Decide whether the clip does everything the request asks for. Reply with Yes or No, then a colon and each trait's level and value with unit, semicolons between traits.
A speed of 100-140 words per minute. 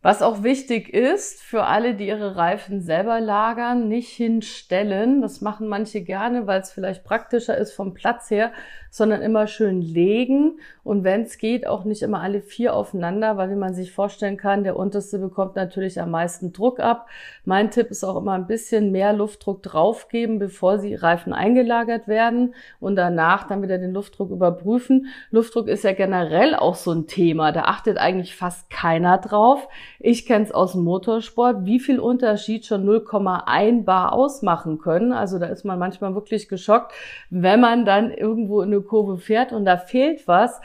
No: average, 180 wpm